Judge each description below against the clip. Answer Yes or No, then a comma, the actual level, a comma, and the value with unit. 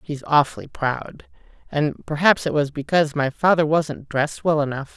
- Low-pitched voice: No, medium, 150 Hz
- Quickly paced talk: No, average, 170 wpm